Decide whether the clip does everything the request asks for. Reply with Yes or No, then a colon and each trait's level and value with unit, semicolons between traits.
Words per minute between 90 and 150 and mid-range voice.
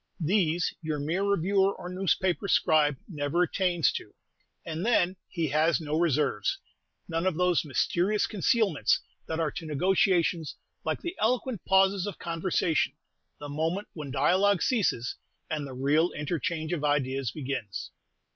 Yes: average, 140 wpm; medium, 165 Hz